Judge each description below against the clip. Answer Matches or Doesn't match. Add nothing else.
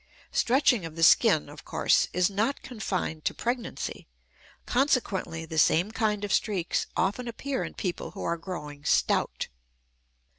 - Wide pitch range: Matches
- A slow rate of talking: Doesn't match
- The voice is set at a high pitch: Matches